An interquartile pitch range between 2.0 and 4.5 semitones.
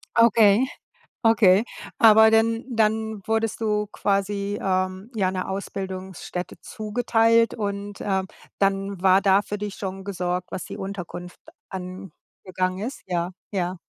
Yes: narrow, 2.6 semitones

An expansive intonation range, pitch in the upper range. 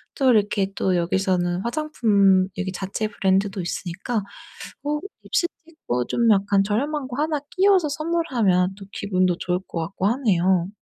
Yes: wide, 6.0 semitones; high, 200 Hz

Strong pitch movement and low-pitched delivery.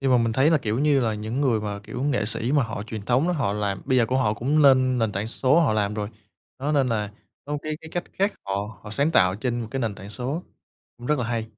No: average, 4.6 semitones; low, 120 Hz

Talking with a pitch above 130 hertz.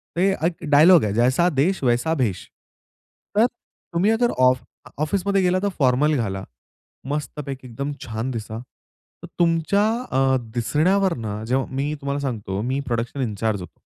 Yes: medium, 140 Hz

